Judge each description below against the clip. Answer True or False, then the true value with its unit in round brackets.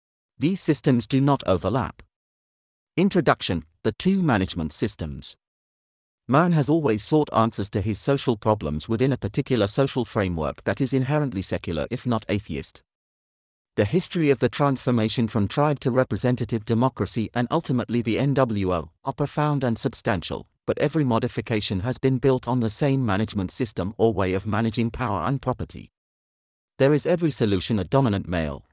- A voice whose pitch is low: True (120 Hz)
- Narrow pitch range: False (5.4 semitones)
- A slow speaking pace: False (155 wpm)